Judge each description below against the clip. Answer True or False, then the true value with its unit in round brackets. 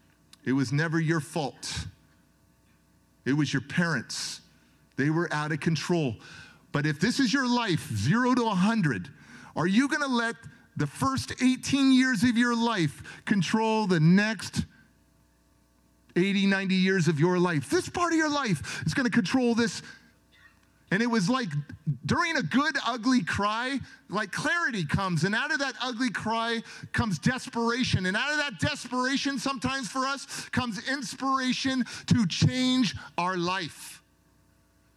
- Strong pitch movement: True (8.2 semitones)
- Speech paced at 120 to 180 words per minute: True (150 wpm)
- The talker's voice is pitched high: True (210 Hz)